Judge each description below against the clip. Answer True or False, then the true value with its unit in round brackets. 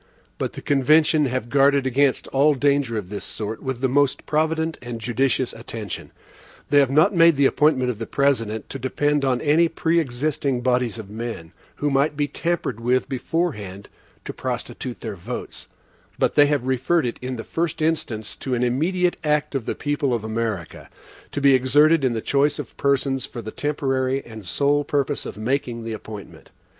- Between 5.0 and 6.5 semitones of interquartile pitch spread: False (3.7 semitones)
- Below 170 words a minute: False (180 wpm)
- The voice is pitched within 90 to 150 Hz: True (135 Hz)